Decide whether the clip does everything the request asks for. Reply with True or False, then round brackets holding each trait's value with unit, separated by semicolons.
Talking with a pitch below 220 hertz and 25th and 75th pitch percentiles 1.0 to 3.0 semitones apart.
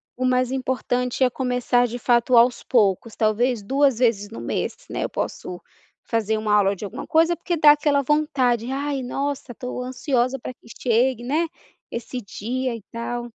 False (250 Hz; 2.4 semitones)